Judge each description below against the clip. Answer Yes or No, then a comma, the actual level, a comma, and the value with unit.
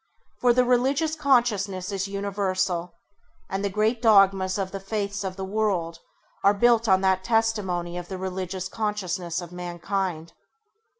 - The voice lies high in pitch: Yes, high, 195 Hz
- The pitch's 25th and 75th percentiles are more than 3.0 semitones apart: No, narrow, 2.6 semitones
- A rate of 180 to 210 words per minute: No, average, 145 wpm